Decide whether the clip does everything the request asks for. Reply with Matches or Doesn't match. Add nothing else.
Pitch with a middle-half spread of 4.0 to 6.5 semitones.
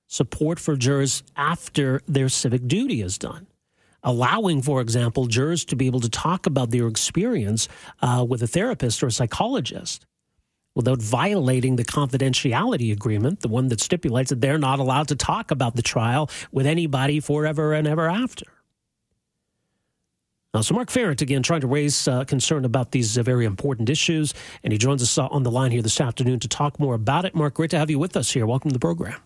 Doesn't match